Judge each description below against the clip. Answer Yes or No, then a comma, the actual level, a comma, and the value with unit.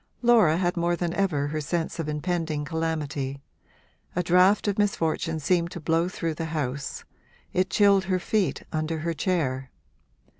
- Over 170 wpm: No, average, 155 wpm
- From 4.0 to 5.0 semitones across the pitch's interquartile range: No, average, 2.9 semitones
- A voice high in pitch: No, medium, 165 Hz